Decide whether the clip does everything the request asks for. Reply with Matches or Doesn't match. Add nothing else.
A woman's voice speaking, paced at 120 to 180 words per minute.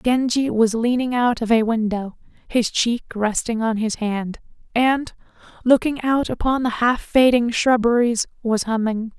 Matches